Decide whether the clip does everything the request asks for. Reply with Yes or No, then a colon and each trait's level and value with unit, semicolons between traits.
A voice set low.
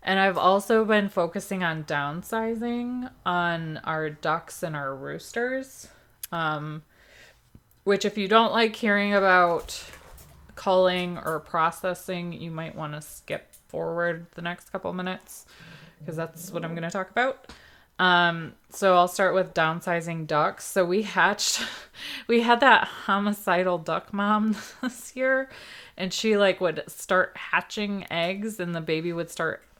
No: medium, 180 Hz